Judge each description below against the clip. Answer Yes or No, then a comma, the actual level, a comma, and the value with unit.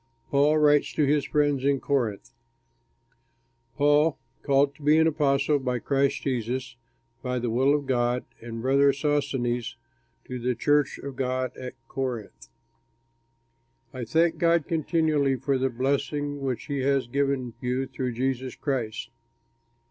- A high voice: No, low, 135 Hz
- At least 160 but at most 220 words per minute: No, average, 140 wpm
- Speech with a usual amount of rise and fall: No, narrow, 2.3 semitones